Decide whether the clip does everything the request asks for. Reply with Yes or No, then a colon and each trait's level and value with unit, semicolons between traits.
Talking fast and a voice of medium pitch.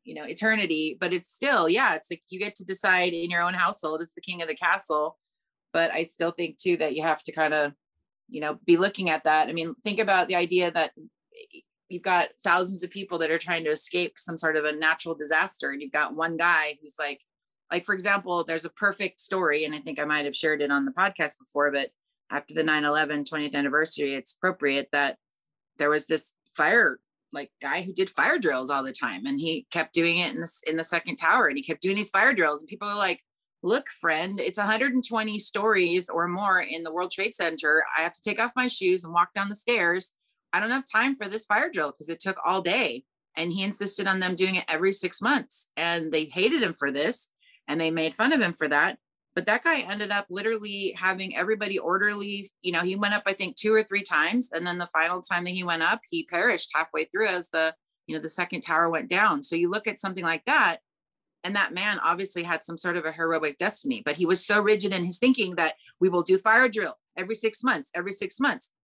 Yes: fast, 240 wpm; medium, 175 Hz